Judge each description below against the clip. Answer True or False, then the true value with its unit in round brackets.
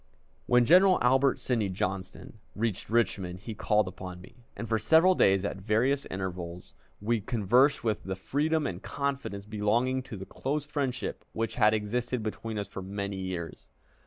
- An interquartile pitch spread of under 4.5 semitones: False (4.9 semitones)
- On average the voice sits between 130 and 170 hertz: False (110 Hz)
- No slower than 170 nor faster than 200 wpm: False (160 wpm)